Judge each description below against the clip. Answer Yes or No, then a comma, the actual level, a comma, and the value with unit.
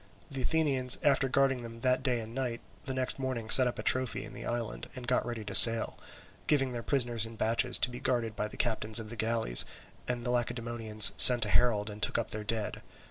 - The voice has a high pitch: No, low, 120 Hz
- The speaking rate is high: Yes, fast, 225 wpm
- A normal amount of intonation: No, narrow, 2.2 semitones